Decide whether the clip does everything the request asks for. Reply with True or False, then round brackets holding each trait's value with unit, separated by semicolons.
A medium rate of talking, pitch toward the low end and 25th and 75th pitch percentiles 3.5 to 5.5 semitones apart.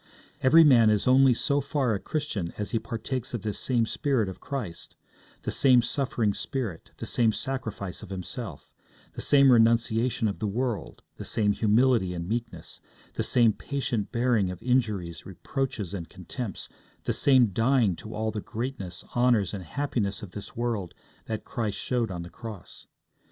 True (165 wpm; 115 Hz; 4.3 semitones)